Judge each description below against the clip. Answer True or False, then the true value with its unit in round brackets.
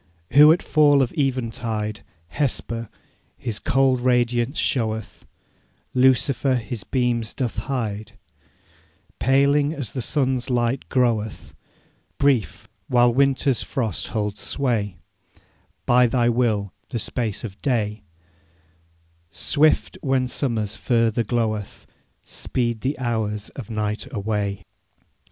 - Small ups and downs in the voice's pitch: False (3.4 semitones)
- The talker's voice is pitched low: True (120 Hz)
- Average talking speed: False (105 wpm)